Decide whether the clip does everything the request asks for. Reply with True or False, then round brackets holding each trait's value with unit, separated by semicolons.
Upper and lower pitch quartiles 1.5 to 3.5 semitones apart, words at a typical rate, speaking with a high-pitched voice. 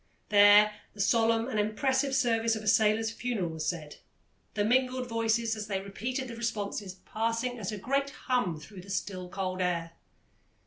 True (3.1 semitones; 170 wpm; 215 Hz)